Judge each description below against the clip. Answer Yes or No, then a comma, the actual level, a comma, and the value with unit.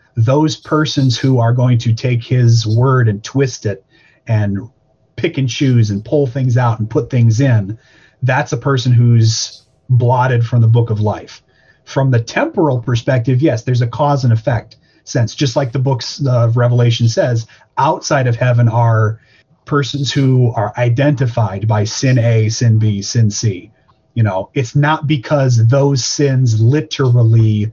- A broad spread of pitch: No, average, 3.1 semitones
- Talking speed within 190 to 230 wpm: No, average, 160 wpm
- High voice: No, low, 125 Hz